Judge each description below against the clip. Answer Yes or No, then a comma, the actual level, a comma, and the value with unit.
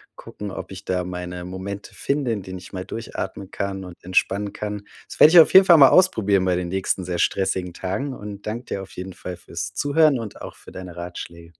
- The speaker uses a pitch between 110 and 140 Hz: No, very low, 95 Hz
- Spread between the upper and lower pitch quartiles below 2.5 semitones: No, average, 2.8 semitones